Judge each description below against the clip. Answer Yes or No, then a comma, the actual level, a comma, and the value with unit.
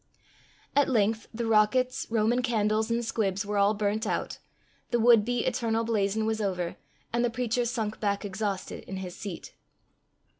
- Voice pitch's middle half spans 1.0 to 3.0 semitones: Yes, narrow, 2.5 semitones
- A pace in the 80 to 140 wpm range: No, average, 160 wpm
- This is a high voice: Yes, high, 220 Hz